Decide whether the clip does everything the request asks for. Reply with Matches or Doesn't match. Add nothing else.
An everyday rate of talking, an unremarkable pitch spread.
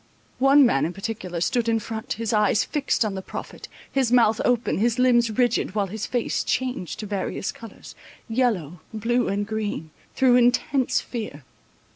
Matches